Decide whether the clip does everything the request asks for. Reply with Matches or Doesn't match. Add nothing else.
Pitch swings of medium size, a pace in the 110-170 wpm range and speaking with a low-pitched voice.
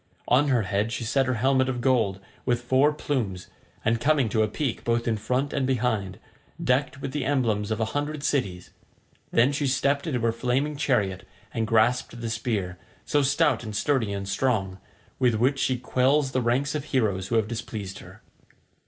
Doesn't match